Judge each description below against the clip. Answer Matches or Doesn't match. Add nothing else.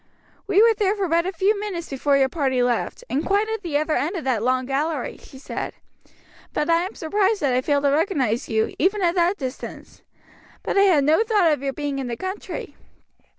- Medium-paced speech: Doesn't match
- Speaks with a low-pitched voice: Doesn't match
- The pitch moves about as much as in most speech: Doesn't match